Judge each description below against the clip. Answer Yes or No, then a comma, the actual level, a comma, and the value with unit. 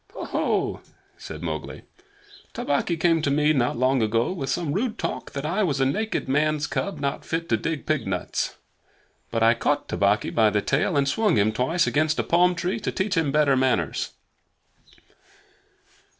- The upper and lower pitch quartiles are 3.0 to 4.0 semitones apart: No, average, 4.9 semitones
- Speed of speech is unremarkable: Yes, average, 180 wpm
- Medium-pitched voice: Yes, medium, 145 Hz